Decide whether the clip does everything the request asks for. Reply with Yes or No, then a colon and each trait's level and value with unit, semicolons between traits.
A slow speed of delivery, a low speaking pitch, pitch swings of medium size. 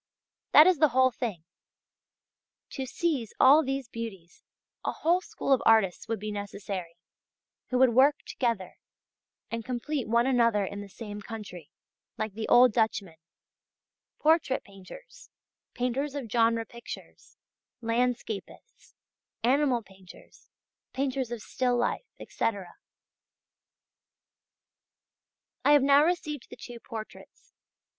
No: slow, 120 wpm; high, 235 Hz; average, 4.1 semitones